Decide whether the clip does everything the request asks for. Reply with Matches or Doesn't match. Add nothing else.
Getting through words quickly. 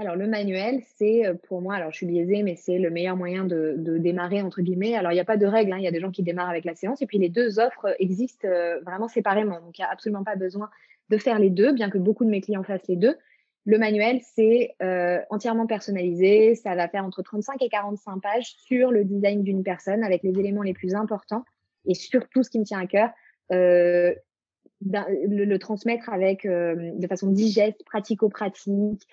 Matches